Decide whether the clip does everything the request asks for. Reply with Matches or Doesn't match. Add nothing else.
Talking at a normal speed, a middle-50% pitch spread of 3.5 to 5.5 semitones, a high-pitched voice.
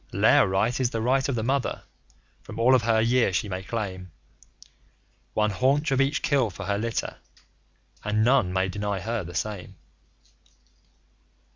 Doesn't match